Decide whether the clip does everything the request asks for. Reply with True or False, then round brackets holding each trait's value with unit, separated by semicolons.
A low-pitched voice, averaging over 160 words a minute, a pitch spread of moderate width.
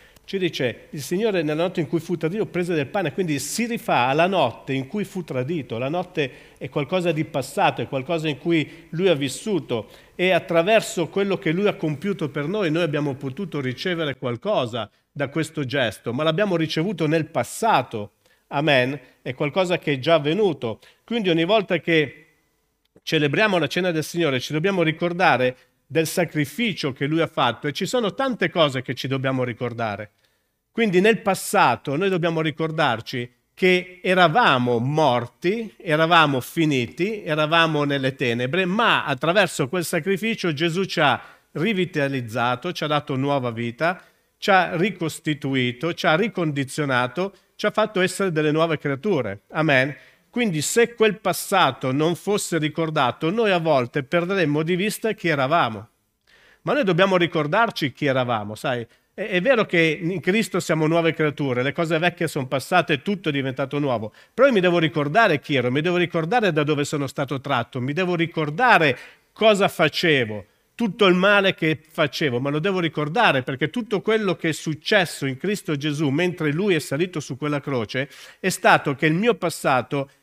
False (160 Hz; 170 wpm; 4.5 semitones)